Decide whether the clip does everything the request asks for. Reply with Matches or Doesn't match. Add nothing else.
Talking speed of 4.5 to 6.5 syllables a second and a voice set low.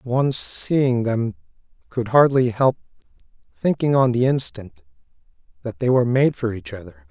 Matches